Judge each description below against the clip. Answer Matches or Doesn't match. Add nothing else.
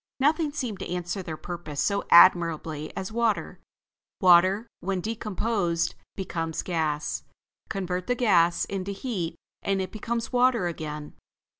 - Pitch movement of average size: Matches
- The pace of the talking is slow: Matches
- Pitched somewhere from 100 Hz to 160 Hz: Doesn't match